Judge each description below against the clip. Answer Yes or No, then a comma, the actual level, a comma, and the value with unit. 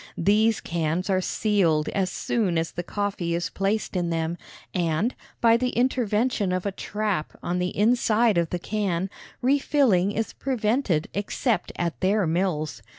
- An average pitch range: Yes, average, 4.1 semitones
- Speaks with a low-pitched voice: No, high, 195 Hz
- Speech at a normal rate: Yes, average, 155 wpm